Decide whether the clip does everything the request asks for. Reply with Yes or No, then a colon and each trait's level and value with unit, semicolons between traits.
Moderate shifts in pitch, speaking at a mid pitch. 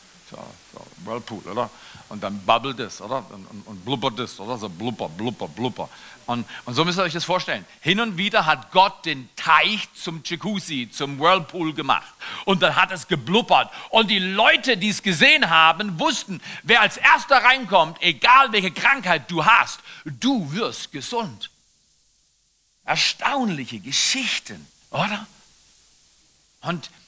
No: wide, 6.8 semitones; medium, 180 Hz